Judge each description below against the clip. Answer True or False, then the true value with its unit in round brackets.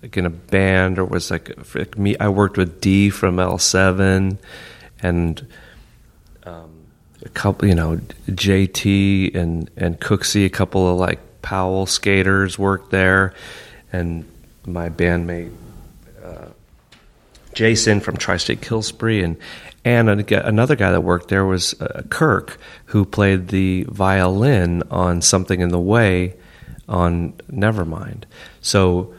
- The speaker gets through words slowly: True (130 wpm)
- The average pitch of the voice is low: True (95 Hz)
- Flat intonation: True (2.3 semitones)